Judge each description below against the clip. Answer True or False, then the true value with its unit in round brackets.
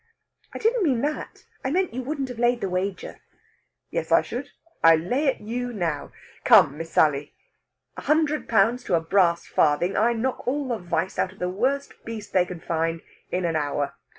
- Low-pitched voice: False (205 Hz)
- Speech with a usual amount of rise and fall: False (7.4 semitones)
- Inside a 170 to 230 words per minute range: True (195 wpm)